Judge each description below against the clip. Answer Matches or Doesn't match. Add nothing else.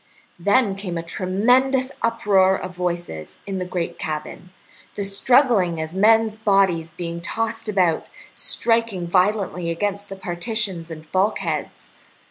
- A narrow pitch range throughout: Doesn't match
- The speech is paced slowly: Matches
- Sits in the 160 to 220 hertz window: Matches